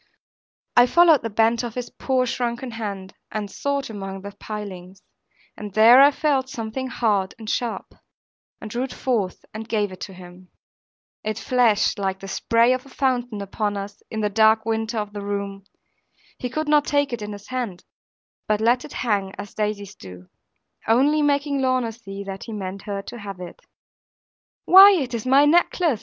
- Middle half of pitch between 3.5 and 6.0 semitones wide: Yes, average, 4.1 semitones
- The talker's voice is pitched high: Yes, high, 220 Hz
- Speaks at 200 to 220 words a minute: No, average, 185 wpm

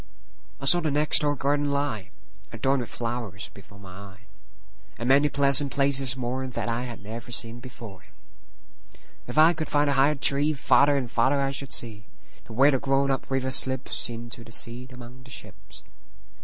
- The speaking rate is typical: Yes, average, 155 wpm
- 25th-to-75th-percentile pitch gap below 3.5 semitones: Yes, average, 3.1 semitones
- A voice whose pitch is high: No, low, 130 Hz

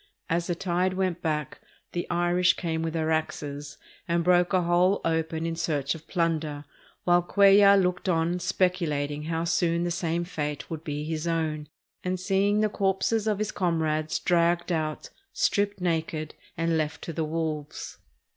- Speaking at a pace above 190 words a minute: No, average, 165 wpm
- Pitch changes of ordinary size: No, narrow, 2.3 semitones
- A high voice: No, medium, 170 Hz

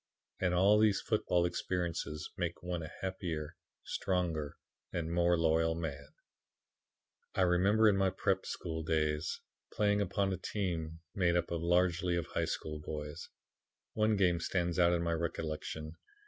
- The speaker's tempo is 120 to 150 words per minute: Yes, average, 145 wpm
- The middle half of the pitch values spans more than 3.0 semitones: No, narrow, 2.5 semitones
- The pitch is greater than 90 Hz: No, very low, 85 Hz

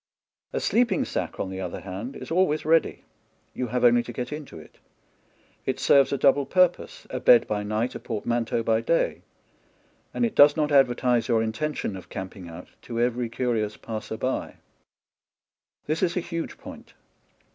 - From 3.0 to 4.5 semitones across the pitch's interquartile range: No, average, 5.1 semitones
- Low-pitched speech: Yes, low, 125 Hz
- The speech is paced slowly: No, average, 180 wpm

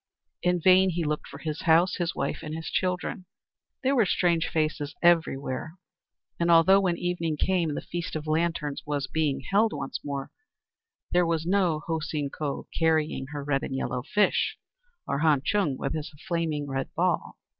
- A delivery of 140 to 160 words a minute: No, average, 175 wpm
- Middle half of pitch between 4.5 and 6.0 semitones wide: No, average, 3.0 semitones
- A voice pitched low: No, medium, 160 Hz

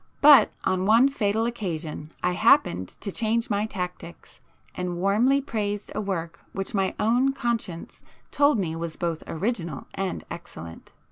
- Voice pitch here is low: No, high, 195 Hz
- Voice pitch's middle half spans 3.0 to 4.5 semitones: No, average, 5.2 semitones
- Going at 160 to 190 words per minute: No, average, 145 wpm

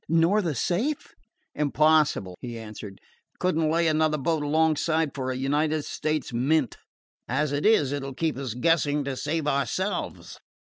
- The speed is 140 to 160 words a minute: Yes, average, 155 wpm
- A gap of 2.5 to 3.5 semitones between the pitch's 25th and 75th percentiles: Yes, average, 3.0 semitones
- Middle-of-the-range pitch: Yes, medium, 150 Hz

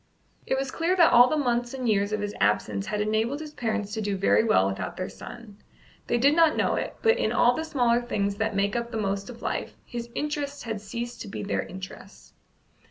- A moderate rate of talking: No, fast, 230 wpm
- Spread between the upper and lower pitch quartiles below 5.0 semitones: Yes, average, 4.3 semitones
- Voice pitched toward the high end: Yes, high, 230 Hz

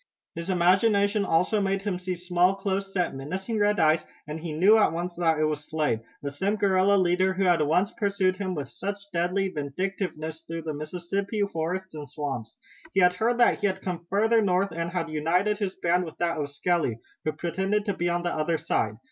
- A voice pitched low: No, medium, 180 Hz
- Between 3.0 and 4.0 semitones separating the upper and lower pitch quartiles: Yes, average, 3.4 semitones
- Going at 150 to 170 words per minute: No, fast, 205 wpm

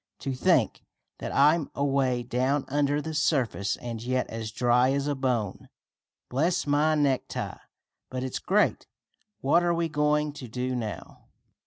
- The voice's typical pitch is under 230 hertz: Yes, low, 135 Hz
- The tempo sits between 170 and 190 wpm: No, average, 150 wpm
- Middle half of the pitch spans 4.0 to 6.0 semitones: No, average, 3.0 semitones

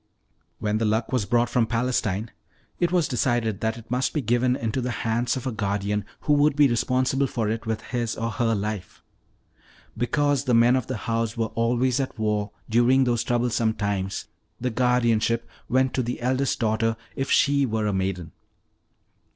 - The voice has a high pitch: No, low, 115 Hz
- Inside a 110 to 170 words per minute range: No, average, 180 wpm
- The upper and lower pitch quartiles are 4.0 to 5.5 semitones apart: No, narrow, 2.5 semitones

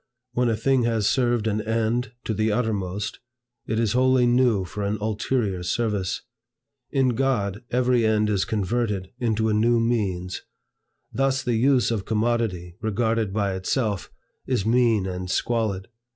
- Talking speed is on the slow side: No, average, 150 wpm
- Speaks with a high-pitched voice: No, low, 110 Hz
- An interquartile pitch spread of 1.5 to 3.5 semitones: Yes, average, 3.0 semitones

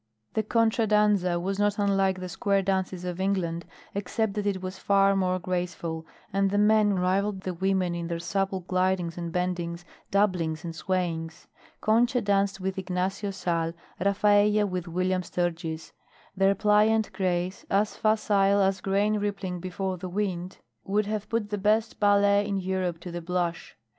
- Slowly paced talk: No, average, 160 wpm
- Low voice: No, high, 190 Hz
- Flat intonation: Yes, narrow, 2.3 semitones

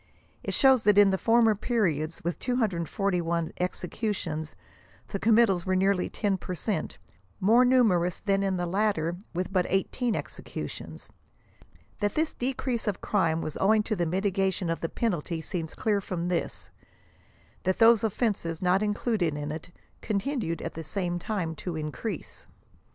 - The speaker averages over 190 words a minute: No, average, 155 wpm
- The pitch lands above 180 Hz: Yes, high, 190 Hz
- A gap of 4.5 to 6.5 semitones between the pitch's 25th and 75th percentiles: No, average, 4.1 semitones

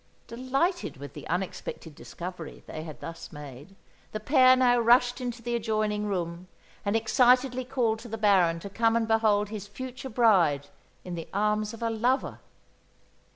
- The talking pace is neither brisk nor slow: Yes, average, 160 wpm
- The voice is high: Yes, high, 215 Hz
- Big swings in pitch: No, average, 4.9 semitones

